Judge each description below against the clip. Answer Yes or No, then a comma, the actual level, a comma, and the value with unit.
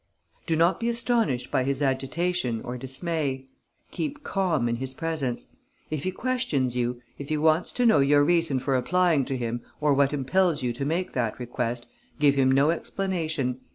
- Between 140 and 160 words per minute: No, average, 180 wpm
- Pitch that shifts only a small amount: No, average, 4.8 semitones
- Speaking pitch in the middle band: Yes, medium, 145 Hz